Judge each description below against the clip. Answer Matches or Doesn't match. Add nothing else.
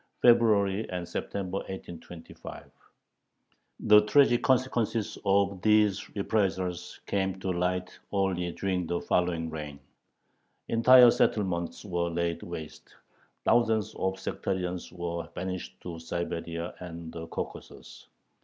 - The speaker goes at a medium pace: Doesn't match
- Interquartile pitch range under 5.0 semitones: Matches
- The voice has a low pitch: Matches